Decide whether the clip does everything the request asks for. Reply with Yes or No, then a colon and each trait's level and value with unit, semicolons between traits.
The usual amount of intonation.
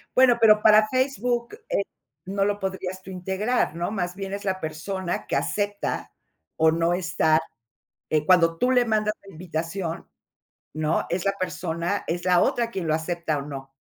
Yes: average, 3.8 semitones